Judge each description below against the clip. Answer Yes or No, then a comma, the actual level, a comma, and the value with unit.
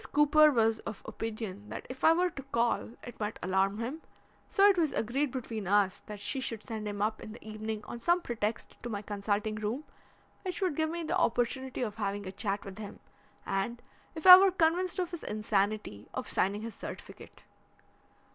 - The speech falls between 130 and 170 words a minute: No, average, 195 wpm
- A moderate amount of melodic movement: No, wide, 6.2 semitones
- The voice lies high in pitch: Yes, high, 225 Hz